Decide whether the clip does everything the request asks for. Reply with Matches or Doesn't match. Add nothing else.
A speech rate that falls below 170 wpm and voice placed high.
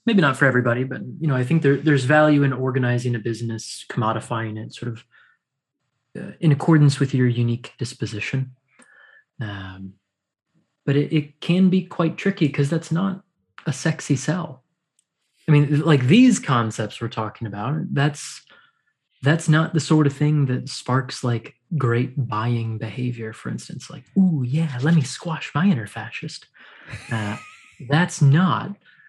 Doesn't match